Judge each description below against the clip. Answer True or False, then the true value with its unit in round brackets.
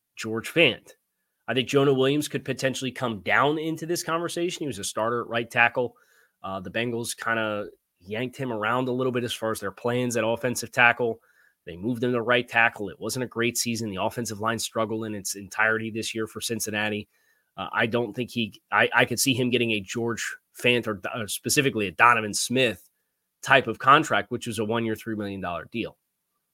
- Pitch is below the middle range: True (115 Hz)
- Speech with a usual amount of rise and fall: False (2.3 semitones)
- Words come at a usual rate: False (210 wpm)